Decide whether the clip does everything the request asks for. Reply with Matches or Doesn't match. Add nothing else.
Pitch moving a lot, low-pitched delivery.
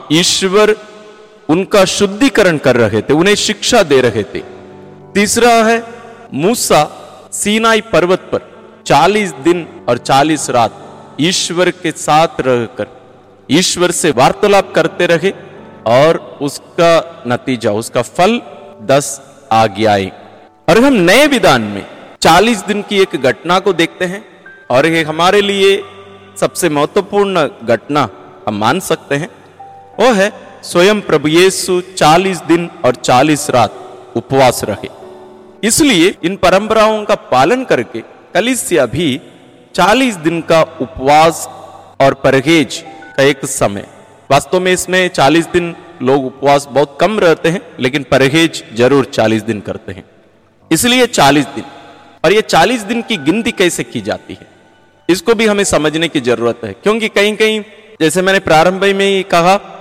Doesn't match